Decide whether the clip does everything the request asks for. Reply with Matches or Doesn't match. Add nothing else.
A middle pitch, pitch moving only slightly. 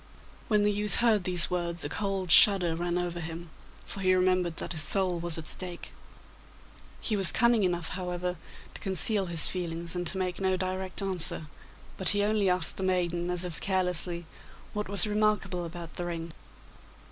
Matches